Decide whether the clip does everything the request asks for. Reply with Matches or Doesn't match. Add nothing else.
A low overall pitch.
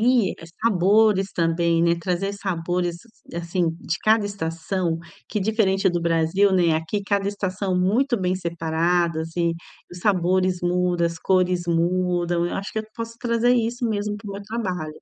Doesn't match